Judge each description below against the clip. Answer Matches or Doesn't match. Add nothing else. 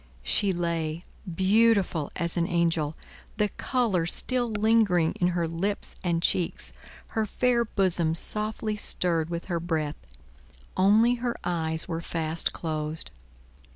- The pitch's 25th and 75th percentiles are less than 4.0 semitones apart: Doesn't match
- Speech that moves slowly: Matches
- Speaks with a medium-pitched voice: Matches